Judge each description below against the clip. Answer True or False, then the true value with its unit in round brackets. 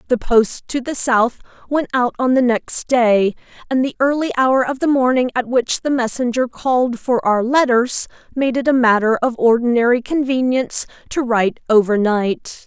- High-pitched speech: True (245 Hz)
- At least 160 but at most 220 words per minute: True (170 wpm)